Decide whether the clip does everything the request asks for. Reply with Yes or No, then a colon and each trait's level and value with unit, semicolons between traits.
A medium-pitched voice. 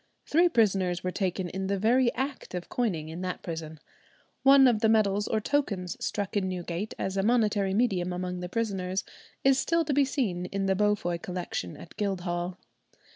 No: high, 195 Hz